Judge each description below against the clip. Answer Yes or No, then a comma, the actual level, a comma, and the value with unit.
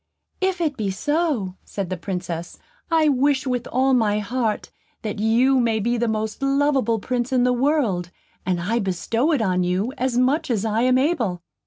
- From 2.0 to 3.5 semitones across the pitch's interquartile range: No, average, 4.7 semitones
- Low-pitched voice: No, high, 235 Hz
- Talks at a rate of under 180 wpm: No, average, 185 wpm